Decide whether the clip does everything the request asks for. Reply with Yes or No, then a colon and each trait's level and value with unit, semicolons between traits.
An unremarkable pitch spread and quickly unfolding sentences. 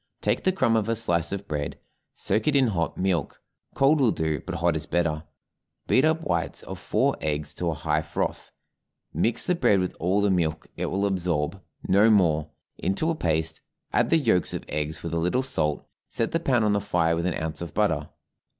No: wide, 5.9 semitones; fast, 210 wpm